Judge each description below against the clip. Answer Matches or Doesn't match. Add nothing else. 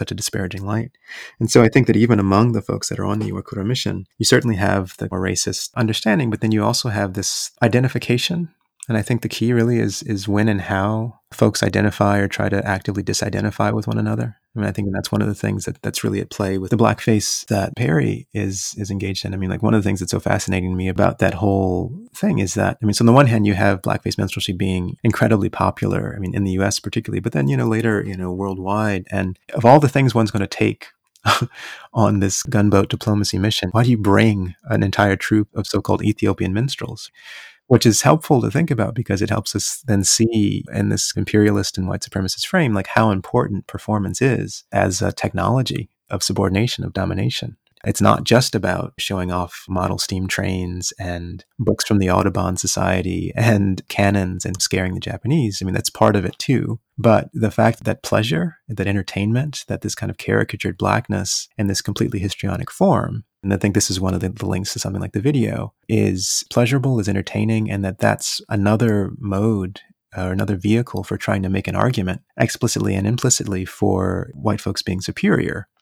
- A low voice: Matches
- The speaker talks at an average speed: Doesn't match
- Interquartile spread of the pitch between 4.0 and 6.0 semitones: Doesn't match